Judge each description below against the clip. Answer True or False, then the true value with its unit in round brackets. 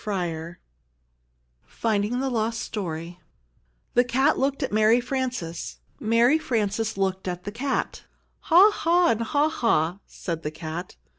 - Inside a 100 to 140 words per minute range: True (135 wpm)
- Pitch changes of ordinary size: False (6.2 semitones)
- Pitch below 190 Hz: False (220 Hz)